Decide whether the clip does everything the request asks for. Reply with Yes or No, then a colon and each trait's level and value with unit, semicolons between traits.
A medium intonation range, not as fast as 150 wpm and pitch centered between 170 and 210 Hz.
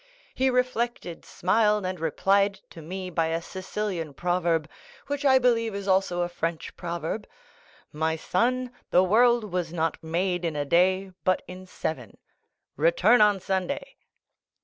Yes: average, 4.0 semitones; average, 140 wpm; medium, 185 Hz